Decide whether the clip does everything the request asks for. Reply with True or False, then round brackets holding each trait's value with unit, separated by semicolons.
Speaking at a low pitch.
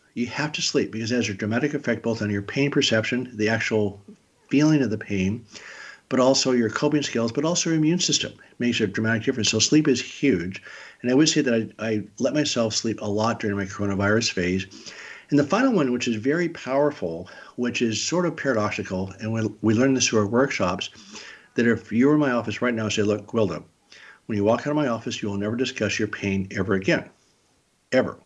True (115 Hz)